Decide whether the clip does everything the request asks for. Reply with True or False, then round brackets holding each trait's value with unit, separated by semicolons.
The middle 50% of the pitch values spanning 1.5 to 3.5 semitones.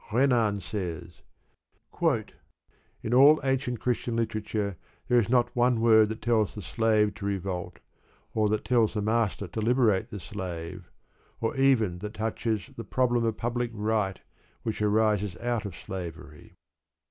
True (2.9 semitones)